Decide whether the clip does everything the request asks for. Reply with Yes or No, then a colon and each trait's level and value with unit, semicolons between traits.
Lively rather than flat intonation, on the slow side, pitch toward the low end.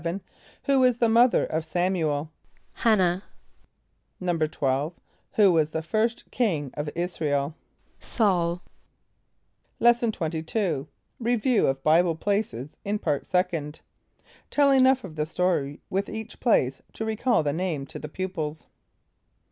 No: wide, 6.2 semitones; slow, 130 wpm; medium, 175 Hz